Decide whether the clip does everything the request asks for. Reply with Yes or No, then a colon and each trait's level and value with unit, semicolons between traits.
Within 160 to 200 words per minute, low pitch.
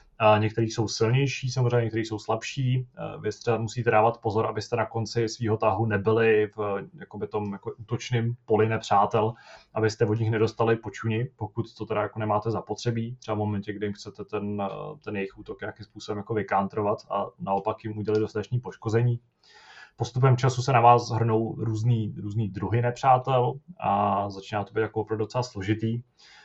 Yes: average, 165 wpm; low, 110 Hz